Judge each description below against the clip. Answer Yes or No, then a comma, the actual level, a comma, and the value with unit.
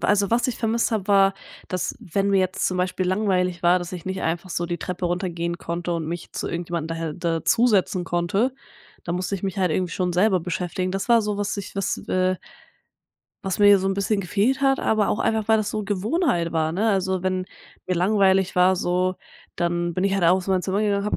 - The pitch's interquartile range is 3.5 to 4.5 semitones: No, narrow, 2.4 semitones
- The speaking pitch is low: No, medium, 185 Hz